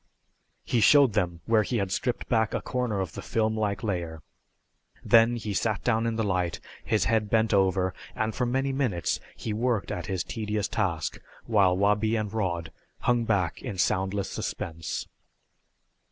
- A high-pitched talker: No, low, 105 Hz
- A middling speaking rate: Yes, average, 170 wpm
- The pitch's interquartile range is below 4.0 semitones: Yes, average, 3.4 semitones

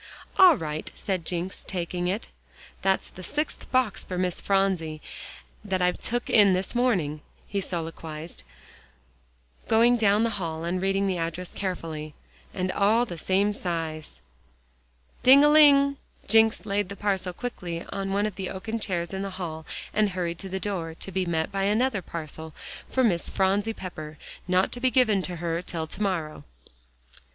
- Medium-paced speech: Yes, average, 165 wpm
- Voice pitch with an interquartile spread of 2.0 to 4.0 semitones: Yes, average, 3.6 semitones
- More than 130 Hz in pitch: Yes, high, 190 Hz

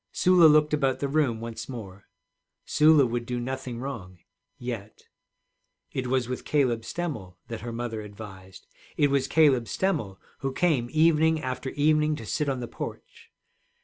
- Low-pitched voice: Yes, low, 130 Hz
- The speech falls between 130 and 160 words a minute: Yes, average, 155 wpm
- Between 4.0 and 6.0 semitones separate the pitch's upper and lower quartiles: Yes, average, 4.7 semitones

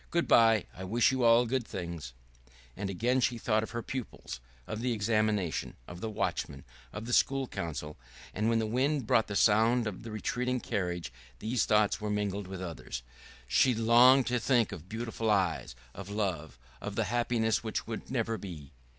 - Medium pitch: No, low, 110 Hz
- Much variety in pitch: No, average, 3.7 semitones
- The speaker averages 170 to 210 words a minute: Yes, average, 185 wpm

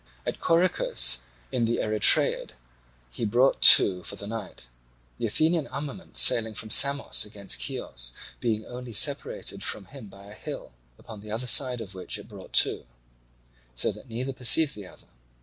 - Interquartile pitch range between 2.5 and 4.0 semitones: No, average, 4.7 semitones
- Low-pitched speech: Yes, low, 115 Hz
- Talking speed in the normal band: Yes, average, 165 wpm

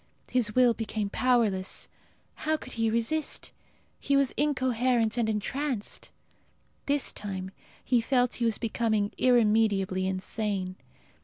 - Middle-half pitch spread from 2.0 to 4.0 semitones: Yes, average, 3.5 semitones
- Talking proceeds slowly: Yes, slow, 115 wpm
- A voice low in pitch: No, high, 230 Hz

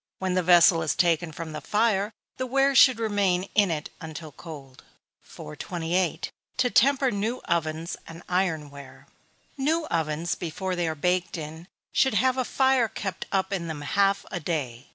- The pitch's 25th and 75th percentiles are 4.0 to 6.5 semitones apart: Yes, average, 4.6 semitones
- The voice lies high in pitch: No, medium, 180 Hz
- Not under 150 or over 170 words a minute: Yes, average, 165 wpm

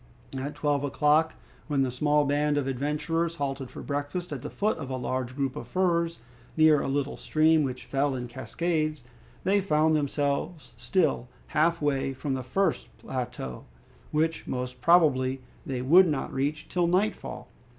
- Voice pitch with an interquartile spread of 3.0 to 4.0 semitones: Yes, average, 3.3 semitones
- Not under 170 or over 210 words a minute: No, average, 160 wpm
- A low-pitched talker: No, medium, 145 Hz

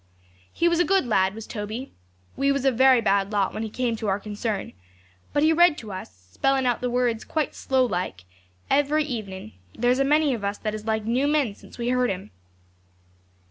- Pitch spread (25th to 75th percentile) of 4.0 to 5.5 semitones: Yes, average, 4.8 semitones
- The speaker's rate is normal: No, fast, 215 wpm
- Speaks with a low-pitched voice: No, high, 240 Hz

